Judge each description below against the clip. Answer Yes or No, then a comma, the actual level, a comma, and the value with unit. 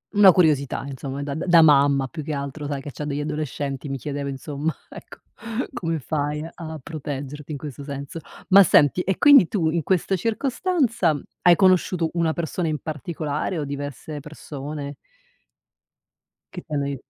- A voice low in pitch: No, medium, 150 Hz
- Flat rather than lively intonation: No, average, 3.1 semitones